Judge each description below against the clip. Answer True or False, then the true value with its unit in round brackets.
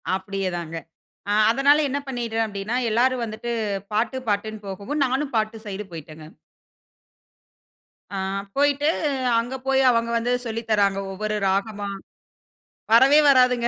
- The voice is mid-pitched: False (225 Hz)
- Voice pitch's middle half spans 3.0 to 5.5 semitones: True (4.2 semitones)